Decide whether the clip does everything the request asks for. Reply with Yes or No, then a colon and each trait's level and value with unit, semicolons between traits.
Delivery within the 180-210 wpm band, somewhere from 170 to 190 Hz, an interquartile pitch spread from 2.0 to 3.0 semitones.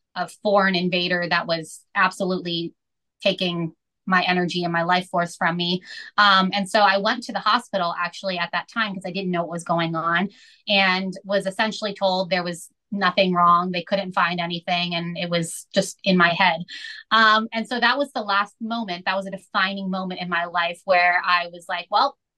Yes: average, 200 wpm; medium, 185 Hz; narrow, 2.4 semitones